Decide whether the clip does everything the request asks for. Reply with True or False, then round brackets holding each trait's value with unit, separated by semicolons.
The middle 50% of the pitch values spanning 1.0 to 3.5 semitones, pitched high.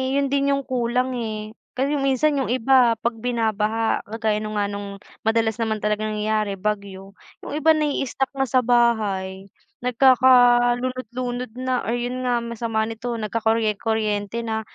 True (2.8 semitones; 230 Hz)